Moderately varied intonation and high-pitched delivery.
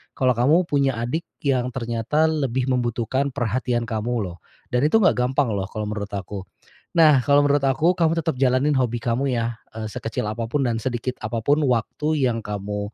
No: average, 3.7 semitones; low, 125 Hz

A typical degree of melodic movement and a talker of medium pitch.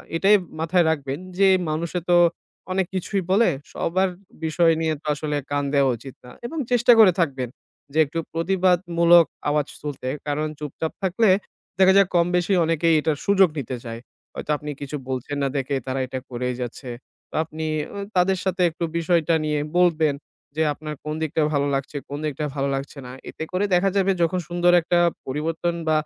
Yes: average, 3.7 semitones; medium, 160 Hz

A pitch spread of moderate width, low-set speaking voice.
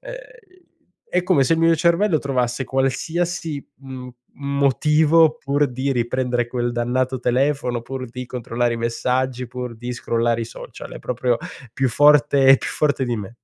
Yes: average, 3.2 semitones; low, 130 Hz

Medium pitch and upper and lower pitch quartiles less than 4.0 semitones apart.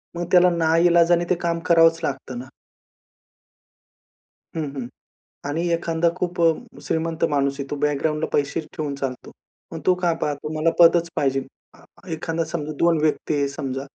Yes: medium, 160 Hz; average, 2.8 semitones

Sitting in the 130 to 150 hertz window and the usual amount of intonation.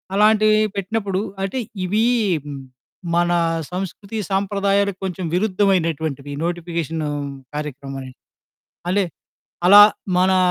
No: medium, 185 Hz; average, 3.5 semitones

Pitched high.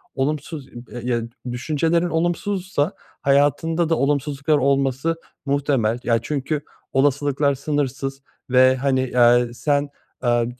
No: medium, 140 Hz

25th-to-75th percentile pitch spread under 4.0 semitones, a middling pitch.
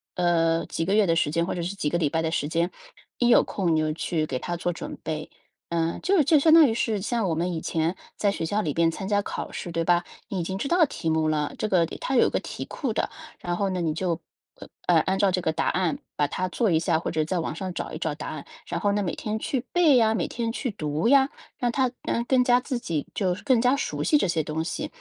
No: wide, 5.4 semitones; medium, 180 Hz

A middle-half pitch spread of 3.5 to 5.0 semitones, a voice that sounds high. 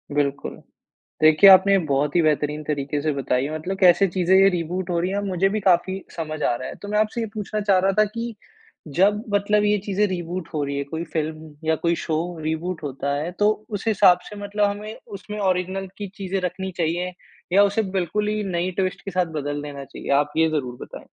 No: average, 4.5 semitones; medium, 180 Hz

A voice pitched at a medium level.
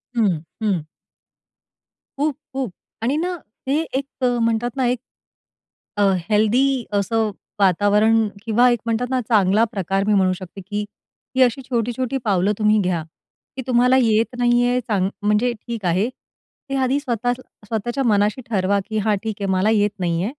No: high, 225 Hz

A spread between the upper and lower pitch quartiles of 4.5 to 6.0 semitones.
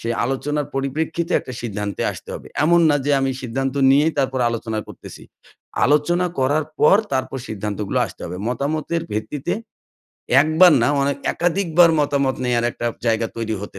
Yes: average, 4.9 semitones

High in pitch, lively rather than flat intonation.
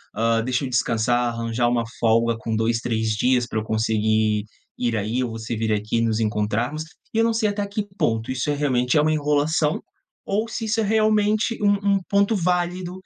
No: low, 125 Hz; wide, 8.7 semitones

